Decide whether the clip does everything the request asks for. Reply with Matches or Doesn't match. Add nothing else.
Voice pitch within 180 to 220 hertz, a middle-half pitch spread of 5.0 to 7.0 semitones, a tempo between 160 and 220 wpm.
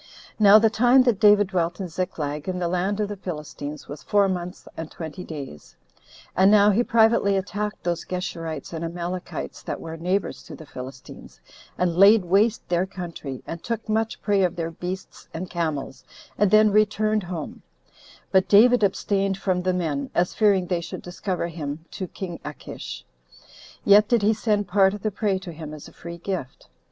Doesn't match